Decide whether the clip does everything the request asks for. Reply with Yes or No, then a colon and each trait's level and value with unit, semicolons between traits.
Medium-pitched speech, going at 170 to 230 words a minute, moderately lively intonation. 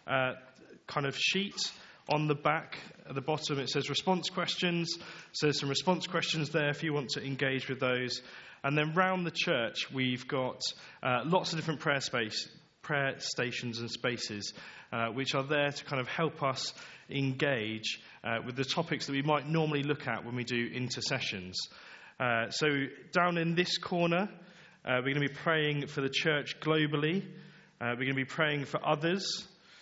Yes: medium, 145 Hz; average, 185 wpm; average, 4.3 semitones